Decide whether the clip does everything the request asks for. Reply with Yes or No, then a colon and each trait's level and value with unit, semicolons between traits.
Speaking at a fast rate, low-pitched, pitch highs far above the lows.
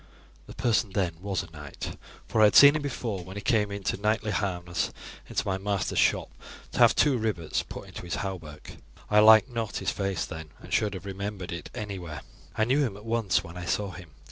No: fast, 215 wpm; low, 100 Hz; average, 3.3 semitones